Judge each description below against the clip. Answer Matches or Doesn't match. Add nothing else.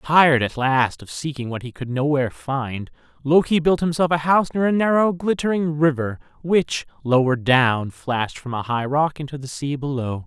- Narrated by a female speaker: Doesn't match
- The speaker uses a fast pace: Doesn't match